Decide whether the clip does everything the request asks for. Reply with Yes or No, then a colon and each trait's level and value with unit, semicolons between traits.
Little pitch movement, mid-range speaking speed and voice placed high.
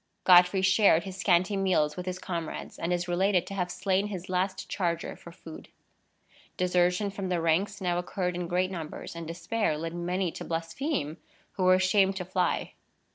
No: narrow, 1.8 semitones; average, 180 wpm; medium, 180 Hz